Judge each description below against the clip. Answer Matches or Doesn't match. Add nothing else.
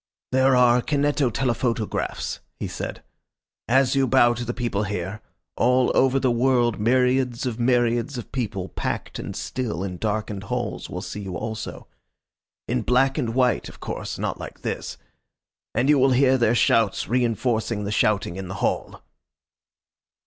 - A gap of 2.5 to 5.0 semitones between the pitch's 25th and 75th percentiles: Matches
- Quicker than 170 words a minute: Doesn't match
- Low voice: Matches